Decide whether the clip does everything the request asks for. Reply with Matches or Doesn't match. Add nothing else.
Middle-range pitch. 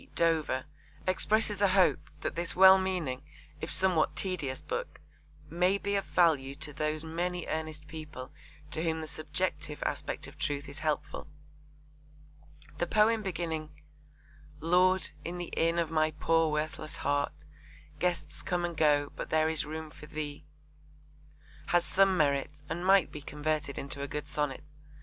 Matches